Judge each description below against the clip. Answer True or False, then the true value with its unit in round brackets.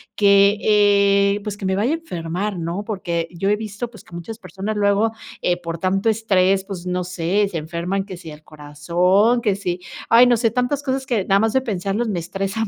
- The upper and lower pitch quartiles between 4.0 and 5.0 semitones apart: False (3.3 semitones)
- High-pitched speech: True (200 Hz)